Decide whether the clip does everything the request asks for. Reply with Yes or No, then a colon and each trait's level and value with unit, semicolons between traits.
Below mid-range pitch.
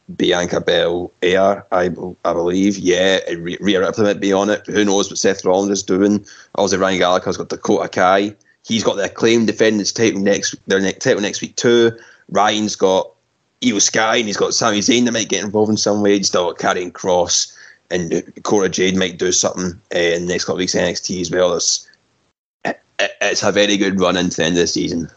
Yes: low, 100 Hz